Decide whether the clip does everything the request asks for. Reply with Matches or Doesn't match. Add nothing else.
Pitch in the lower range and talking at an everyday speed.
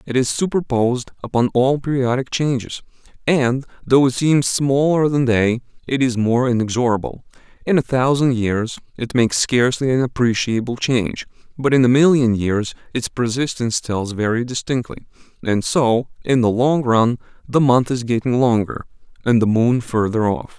Matches